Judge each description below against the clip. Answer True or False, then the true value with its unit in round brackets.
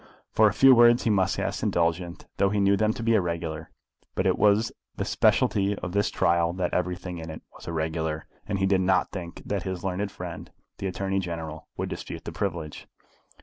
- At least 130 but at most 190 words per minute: False (200 wpm)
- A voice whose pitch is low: True (95 Hz)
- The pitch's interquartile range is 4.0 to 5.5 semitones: False (3.0 semitones)